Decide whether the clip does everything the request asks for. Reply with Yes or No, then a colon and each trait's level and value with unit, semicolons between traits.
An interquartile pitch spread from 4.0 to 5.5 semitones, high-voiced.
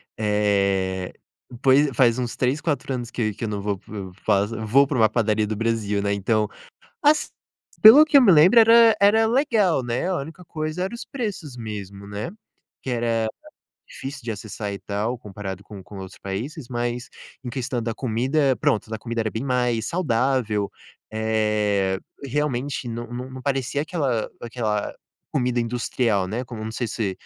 No: average, 4.7 semitones; low, 120 Hz